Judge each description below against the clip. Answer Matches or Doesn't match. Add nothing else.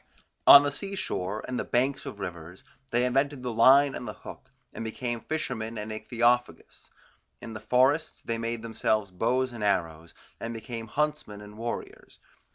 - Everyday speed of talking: Matches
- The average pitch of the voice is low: Matches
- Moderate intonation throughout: Matches